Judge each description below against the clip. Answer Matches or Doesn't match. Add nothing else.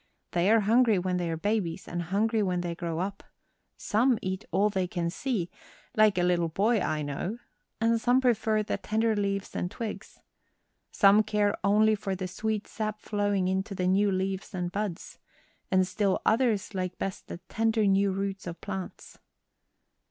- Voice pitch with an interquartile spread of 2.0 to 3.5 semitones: Matches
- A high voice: Matches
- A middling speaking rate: Matches